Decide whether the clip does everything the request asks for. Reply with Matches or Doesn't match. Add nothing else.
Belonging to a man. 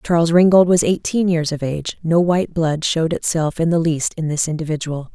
Doesn't match